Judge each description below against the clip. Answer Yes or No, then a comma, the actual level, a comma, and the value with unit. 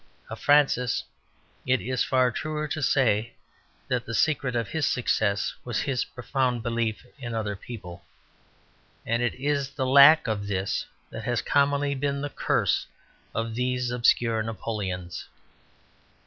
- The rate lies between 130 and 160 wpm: Yes, average, 140 wpm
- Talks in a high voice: No, low, 125 Hz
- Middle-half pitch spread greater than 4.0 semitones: No, average, 3.6 semitones